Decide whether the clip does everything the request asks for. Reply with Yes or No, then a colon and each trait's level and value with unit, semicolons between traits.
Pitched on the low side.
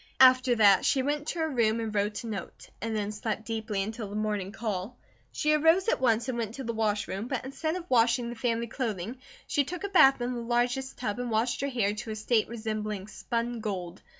No: high, 230 Hz